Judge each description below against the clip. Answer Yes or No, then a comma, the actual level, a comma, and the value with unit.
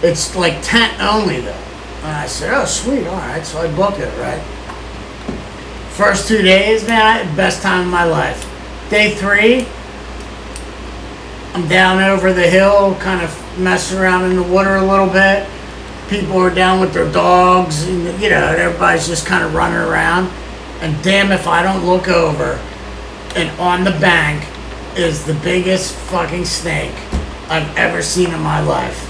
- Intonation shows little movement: Yes, narrow, 2.2 semitones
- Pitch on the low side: No, medium, 185 Hz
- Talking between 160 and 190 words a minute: Yes, average, 165 wpm